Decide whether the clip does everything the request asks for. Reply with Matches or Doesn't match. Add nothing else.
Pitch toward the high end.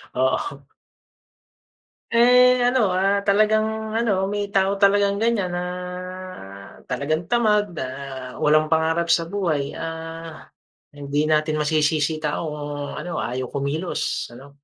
Doesn't match